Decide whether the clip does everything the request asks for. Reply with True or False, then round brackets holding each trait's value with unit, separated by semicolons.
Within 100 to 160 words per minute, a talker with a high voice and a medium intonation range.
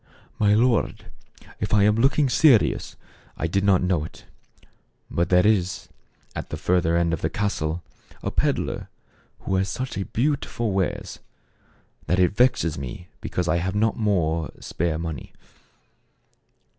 False (145 wpm; 95 Hz; 4.2 semitones)